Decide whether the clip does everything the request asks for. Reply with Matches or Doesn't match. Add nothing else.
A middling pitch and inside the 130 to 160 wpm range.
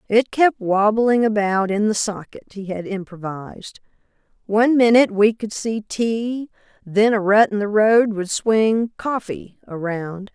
Doesn't match